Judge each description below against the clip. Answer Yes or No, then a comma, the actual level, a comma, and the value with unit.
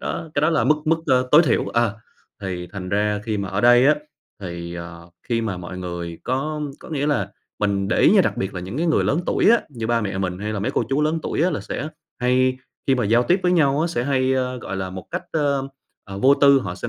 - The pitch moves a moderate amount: No, wide, 6.6 semitones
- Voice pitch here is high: No, low, 120 Hz